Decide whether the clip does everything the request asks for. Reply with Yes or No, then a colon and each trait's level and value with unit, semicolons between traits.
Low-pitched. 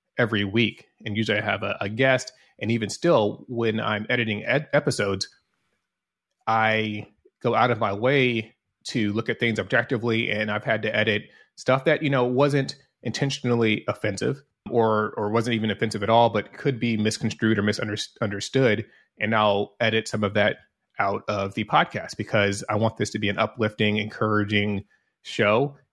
Yes: low, 110 Hz